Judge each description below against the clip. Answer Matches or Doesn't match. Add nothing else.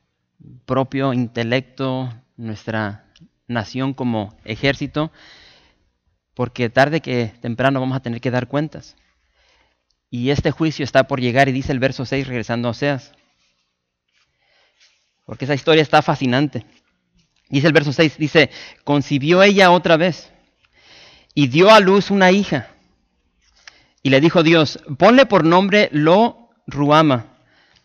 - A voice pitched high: Doesn't match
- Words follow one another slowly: Matches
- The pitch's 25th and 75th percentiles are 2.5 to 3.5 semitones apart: Doesn't match